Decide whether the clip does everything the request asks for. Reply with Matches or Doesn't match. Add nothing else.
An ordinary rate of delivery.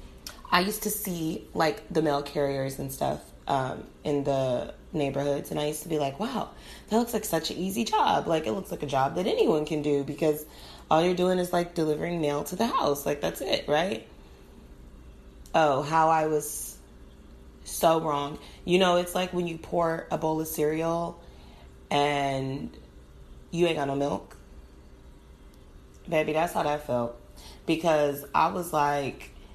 Matches